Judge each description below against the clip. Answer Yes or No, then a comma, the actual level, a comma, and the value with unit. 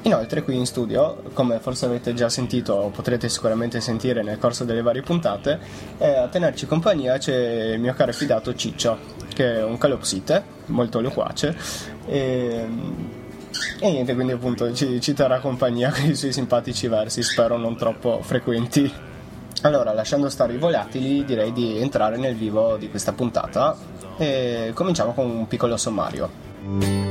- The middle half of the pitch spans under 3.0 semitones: Yes, narrow, 2.5 semitones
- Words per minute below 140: No, average, 155 wpm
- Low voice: Yes, low, 120 Hz